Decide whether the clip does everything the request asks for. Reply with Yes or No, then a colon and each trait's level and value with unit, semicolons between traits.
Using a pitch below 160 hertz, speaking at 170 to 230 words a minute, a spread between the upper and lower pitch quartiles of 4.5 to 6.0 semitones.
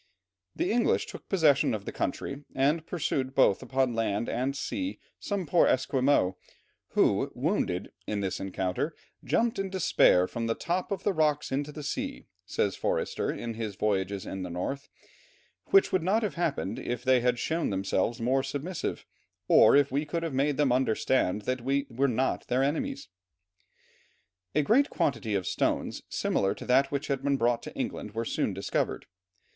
Yes: low, 135 Hz; average, 175 wpm; average, 5.3 semitones